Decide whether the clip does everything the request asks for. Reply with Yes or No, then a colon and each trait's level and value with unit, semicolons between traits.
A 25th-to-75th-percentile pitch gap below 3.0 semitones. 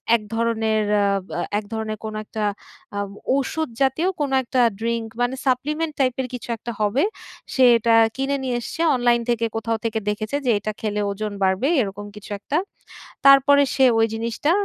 No: average, 3.6 semitones